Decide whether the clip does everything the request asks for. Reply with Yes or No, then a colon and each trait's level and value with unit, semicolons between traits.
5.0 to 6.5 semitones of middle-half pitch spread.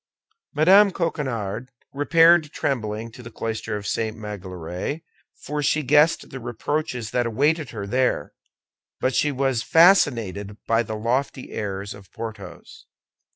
Yes: wide, 5.6 semitones